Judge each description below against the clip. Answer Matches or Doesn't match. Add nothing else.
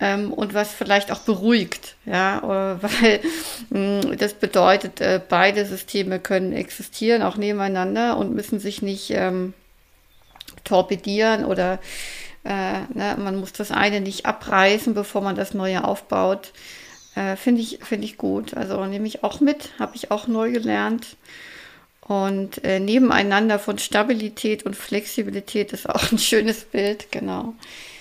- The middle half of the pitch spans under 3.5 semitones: Matches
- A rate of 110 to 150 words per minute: Matches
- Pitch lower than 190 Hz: Doesn't match